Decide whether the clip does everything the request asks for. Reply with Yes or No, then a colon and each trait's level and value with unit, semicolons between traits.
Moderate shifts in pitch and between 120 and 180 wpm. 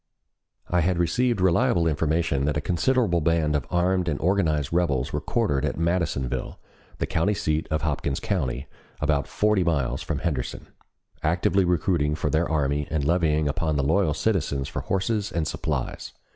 Yes: average, 3.5 semitones; average, 160 wpm